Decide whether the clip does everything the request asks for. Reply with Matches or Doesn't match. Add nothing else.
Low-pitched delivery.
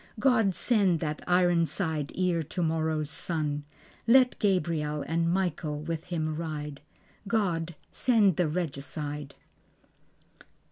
Doesn't match